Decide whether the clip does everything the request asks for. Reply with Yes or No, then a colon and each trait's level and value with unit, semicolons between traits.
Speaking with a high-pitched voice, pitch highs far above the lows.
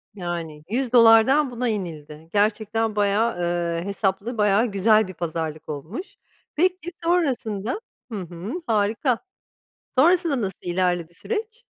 Yes: high, 210 Hz; wide, 6.2 semitones